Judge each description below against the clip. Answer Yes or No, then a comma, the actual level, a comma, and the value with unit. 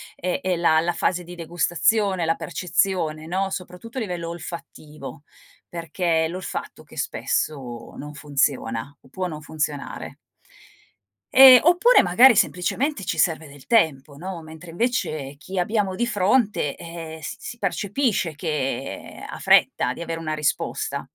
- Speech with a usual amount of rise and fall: Yes, average, 3.8 semitones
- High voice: No, medium, 170 Hz